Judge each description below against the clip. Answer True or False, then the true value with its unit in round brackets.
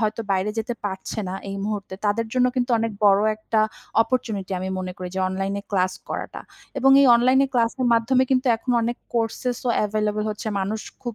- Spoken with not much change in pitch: False (3.6 semitones)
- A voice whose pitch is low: False (220 Hz)